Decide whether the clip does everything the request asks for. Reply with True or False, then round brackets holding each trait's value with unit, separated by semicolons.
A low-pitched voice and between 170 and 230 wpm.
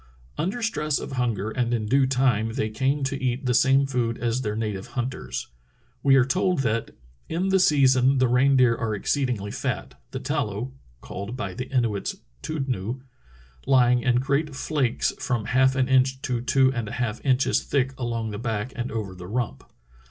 True (125 Hz; 180 wpm)